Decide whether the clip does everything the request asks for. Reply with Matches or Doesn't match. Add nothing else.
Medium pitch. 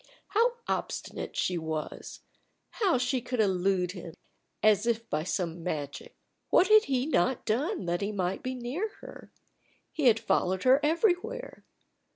Doesn't match